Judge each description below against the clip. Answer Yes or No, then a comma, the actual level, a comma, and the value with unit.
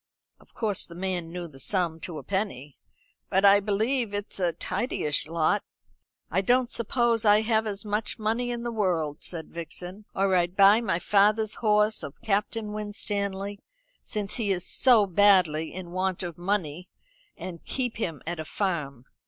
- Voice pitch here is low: No, high, 195 Hz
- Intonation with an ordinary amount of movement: Yes, average, 3.6 semitones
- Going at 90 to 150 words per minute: No, average, 170 wpm